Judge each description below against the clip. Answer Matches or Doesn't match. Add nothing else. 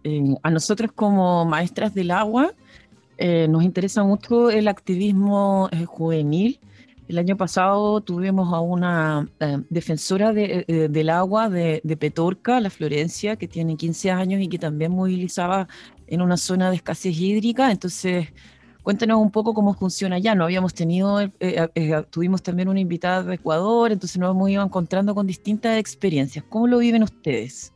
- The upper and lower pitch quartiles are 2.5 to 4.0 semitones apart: Matches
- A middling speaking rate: Matches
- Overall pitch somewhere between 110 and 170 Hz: Doesn't match